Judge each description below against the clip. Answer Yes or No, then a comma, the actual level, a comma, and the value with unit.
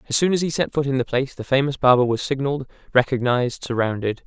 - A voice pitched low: Yes, low, 130 Hz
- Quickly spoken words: Yes, fast, 225 wpm